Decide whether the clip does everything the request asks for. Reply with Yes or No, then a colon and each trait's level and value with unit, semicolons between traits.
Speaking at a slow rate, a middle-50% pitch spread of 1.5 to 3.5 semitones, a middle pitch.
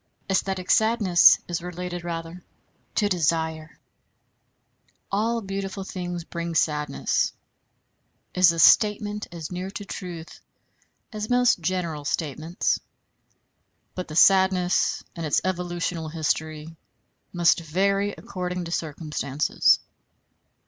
Yes: slow, 100 wpm; average, 2.7 semitones; medium, 175 Hz